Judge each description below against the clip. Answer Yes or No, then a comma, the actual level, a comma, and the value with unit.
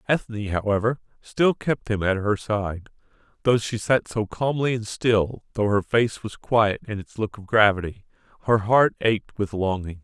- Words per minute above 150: Yes, average, 180 wpm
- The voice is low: Yes, low, 110 Hz